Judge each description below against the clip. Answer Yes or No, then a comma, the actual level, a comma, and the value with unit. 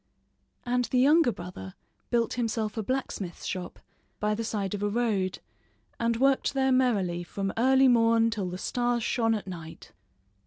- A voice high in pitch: Yes, high, 225 Hz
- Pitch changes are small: No, average, 4.0 semitones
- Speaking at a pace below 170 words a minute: Yes, average, 160 wpm